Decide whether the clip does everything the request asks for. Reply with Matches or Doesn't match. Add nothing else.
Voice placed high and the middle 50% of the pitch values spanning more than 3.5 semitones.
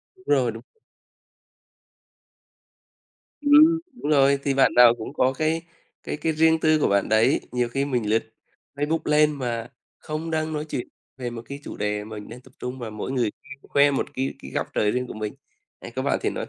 Doesn't match